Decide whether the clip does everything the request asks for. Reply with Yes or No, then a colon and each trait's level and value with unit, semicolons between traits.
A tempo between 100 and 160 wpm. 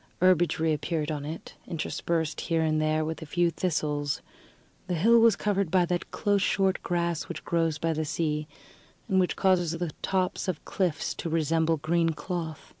No: average, 170 wpm